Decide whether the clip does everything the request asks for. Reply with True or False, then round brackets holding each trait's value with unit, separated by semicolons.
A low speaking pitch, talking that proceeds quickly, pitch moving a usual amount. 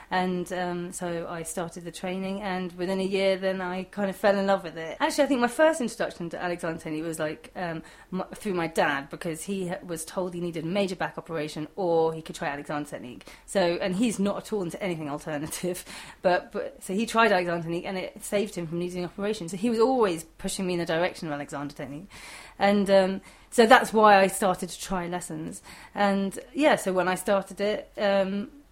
False (185 Hz; 220 wpm; 3.0 semitones)